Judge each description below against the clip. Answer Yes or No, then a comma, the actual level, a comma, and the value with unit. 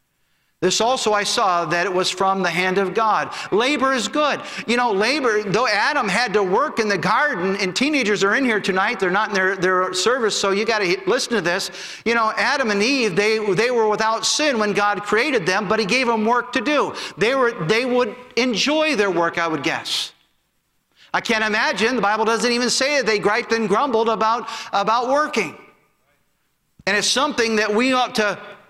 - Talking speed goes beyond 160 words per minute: Yes, fast, 205 wpm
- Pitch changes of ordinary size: Yes, average, 3.7 semitones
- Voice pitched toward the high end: Yes, high, 220 Hz